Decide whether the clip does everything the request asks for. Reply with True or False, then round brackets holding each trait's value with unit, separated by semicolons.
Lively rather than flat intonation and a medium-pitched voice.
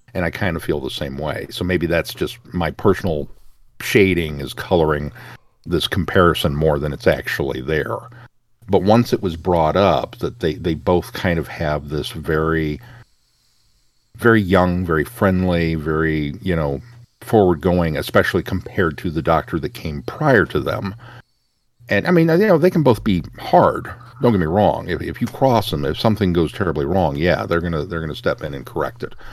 False (6.3 semitones; 90 Hz)